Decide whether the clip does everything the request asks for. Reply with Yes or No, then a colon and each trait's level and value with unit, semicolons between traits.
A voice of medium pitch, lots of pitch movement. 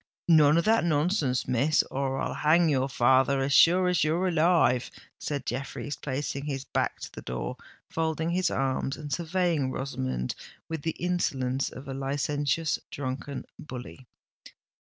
No: medium, 145 Hz; average, 3.6 semitones